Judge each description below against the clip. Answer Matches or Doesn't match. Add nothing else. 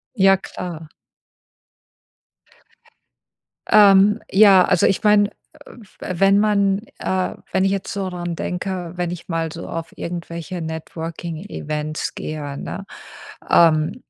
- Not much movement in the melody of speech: Doesn't match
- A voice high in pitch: Doesn't match